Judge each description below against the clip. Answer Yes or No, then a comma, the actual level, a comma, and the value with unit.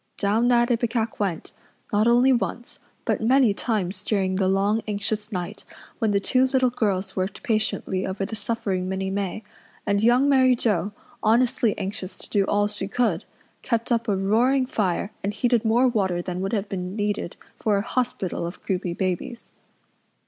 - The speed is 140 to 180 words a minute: Yes, average, 170 wpm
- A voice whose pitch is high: Yes, high, 210 Hz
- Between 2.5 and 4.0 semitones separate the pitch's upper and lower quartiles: Yes, average, 3.6 semitones